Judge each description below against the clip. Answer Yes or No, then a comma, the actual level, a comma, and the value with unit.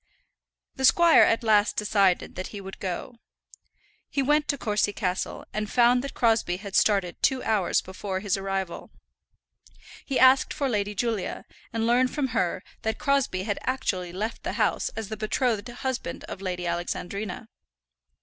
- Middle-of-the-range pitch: No, high, 215 Hz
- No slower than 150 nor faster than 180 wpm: Yes, average, 160 wpm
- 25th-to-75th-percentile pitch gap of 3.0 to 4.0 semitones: No, average, 4.4 semitones